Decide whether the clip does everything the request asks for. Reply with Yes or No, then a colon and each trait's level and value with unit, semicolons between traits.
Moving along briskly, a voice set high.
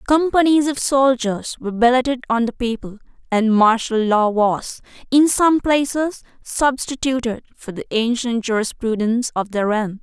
No: average, 140 wpm; high, 240 Hz